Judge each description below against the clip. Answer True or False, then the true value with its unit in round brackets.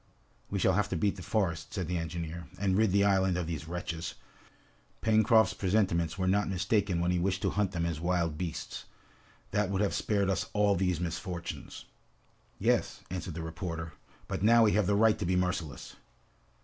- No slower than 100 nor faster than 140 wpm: False (190 wpm)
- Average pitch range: True (3.0 semitones)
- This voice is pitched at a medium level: False (90 Hz)